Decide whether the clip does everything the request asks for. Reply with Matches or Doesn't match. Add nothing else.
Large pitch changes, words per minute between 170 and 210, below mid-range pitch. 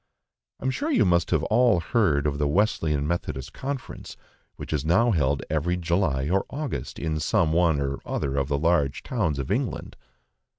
Matches